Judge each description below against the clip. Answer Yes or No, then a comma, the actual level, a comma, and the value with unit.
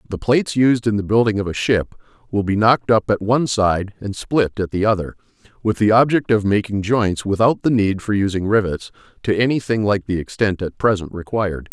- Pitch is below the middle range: Yes, low, 105 Hz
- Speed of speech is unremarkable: No, fast, 210 wpm